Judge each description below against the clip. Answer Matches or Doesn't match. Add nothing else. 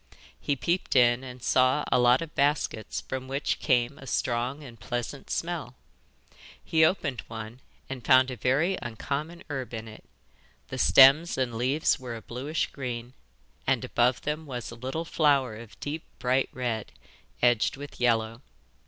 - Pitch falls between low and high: Doesn't match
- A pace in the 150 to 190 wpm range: Matches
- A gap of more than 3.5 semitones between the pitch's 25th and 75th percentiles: Doesn't match